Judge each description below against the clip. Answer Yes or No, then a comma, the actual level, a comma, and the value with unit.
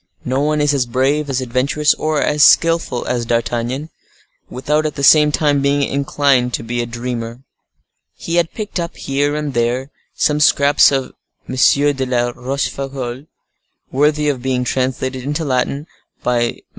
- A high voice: No, low, 135 Hz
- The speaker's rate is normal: Yes, average, 160 wpm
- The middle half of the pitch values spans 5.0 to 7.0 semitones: No, average, 2.9 semitones